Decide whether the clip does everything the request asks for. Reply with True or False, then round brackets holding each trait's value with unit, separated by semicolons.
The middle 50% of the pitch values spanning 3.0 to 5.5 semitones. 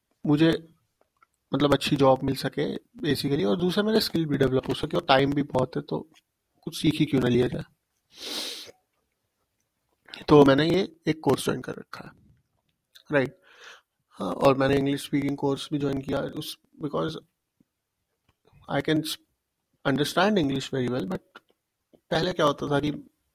False (2.6 semitones)